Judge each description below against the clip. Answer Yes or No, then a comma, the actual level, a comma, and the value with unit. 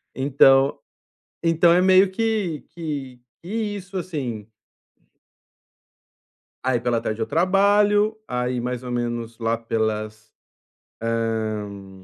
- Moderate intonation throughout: No, wide, 8.1 semitones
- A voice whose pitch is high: No, low, 130 Hz